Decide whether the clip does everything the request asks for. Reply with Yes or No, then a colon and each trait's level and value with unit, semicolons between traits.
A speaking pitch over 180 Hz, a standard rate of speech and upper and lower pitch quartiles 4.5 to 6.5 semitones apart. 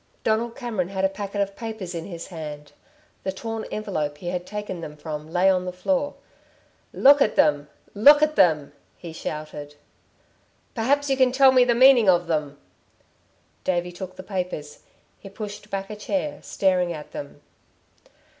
Yes: high, 190 Hz; average, 165 wpm; average, 5.1 semitones